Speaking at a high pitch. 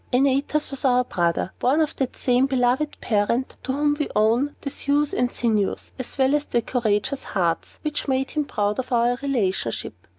Yes: very high, 255 Hz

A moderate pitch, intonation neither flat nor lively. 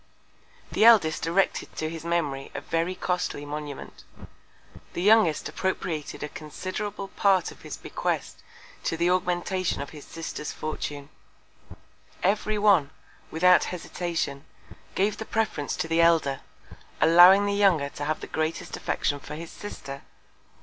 Yes: medium, 170 Hz; average, 3.8 semitones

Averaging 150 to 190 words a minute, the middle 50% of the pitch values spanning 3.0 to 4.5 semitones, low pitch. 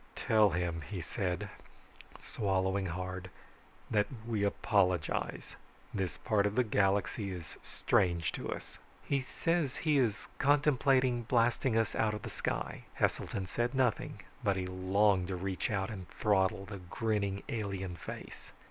No: average, 140 wpm; average, 3.5 semitones; low, 100 Hz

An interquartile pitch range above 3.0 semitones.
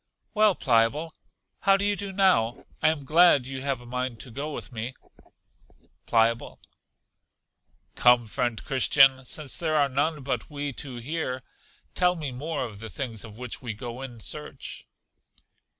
Yes: average, 4.2 semitones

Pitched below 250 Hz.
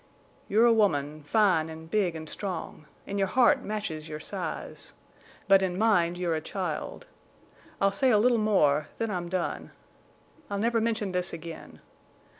Yes: high, 190 Hz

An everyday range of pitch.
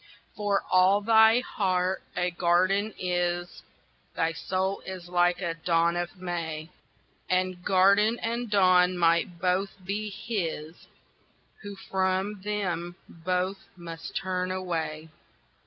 No: narrow, 2.1 semitones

